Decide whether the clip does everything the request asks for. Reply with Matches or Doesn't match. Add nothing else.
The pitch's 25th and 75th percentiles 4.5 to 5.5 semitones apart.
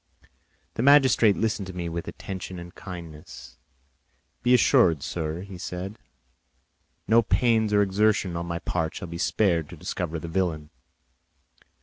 Doesn't match